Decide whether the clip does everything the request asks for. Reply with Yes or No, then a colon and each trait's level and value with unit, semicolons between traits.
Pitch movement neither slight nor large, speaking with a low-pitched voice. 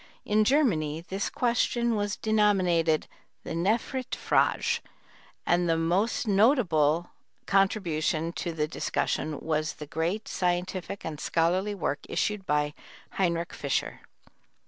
No: average, 4.5 semitones; medium, 175 Hz